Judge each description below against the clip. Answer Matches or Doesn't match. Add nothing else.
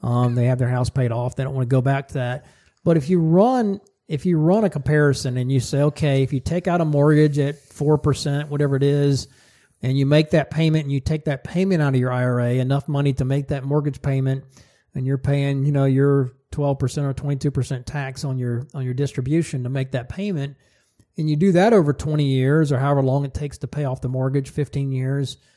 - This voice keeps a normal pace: Doesn't match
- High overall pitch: Doesn't match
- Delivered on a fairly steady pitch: Matches